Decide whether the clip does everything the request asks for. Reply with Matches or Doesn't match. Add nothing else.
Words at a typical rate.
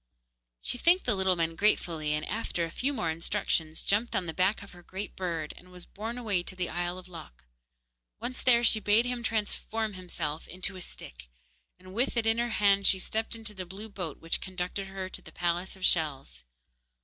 Doesn't match